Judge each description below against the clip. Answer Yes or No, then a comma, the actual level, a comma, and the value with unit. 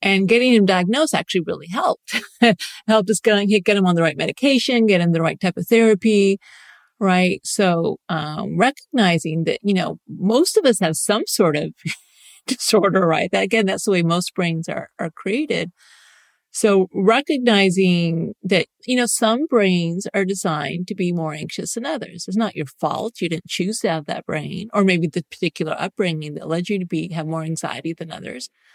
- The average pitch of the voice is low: No, high, 195 Hz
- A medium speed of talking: Yes, average, 190 wpm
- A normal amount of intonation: Yes, average, 4.2 semitones